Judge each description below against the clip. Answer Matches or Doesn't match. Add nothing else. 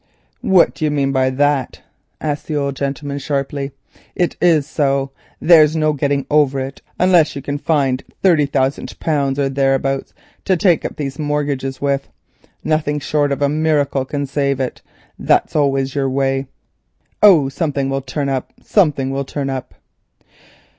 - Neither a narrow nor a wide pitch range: Doesn't match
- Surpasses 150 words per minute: Matches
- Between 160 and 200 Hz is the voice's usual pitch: Doesn't match